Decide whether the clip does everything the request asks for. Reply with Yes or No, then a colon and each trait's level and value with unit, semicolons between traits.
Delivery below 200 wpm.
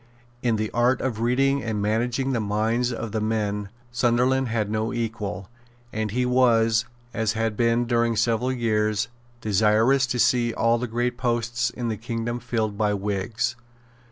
Yes: average, 160 wpm